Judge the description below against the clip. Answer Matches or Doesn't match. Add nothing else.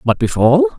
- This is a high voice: Doesn't match